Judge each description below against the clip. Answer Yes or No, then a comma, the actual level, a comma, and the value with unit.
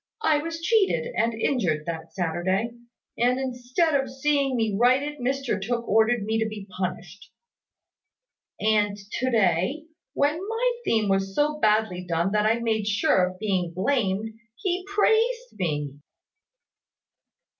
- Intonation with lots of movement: Yes, wide, 6.3 semitones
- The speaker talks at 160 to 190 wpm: No, slow, 135 wpm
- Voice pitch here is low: No, high, 225 Hz